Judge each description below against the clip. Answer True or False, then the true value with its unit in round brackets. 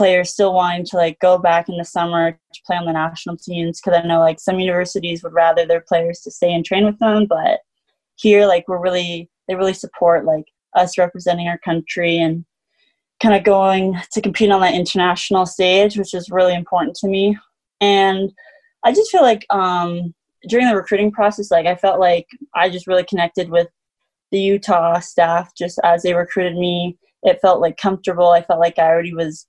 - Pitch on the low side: False (180 Hz)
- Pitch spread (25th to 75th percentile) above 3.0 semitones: False (2.4 semitones)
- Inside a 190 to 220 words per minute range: True (200 wpm)